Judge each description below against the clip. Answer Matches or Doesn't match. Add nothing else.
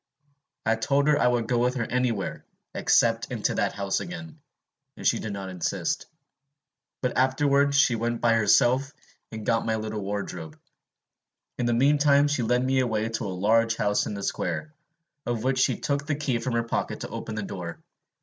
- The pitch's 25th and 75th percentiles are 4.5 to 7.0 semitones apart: Doesn't match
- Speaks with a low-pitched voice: Matches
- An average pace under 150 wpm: Doesn't match